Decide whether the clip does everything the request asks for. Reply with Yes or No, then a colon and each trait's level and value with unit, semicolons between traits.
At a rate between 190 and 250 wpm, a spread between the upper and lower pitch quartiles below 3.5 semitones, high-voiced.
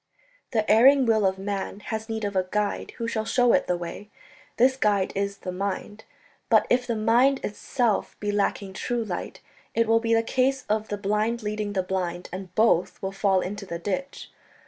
Yes: average, 195 wpm; average, 2.9 semitones; high, 210 Hz